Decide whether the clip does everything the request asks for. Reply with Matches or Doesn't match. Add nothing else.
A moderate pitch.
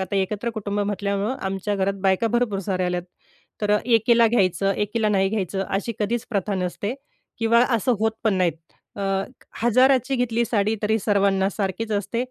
Doesn't match